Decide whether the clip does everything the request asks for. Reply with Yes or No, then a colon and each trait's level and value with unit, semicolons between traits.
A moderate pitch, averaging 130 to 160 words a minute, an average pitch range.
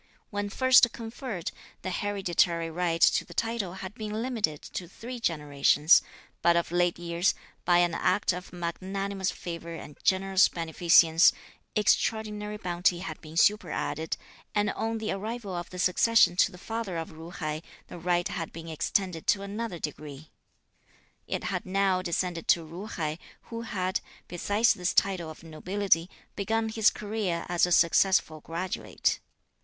Yes: medium, 180 Hz; average, 150 wpm; average, 3.5 semitones